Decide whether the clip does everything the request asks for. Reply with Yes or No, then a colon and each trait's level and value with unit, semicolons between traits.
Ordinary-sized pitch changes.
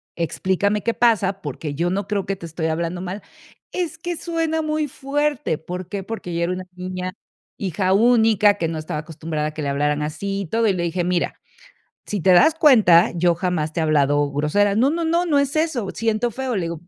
No: wide, 5.9 semitones